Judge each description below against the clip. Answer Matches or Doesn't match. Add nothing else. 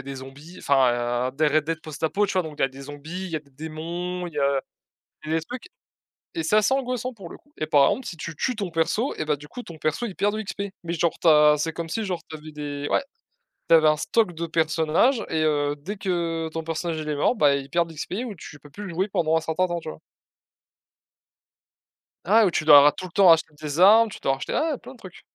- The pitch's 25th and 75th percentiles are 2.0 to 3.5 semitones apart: Doesn't match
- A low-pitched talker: Doesn't match